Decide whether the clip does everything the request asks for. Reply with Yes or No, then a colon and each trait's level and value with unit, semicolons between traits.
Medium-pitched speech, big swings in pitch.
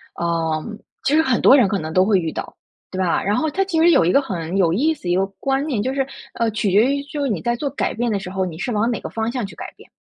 No: high, 220 Hz; wide, 6.6 semitones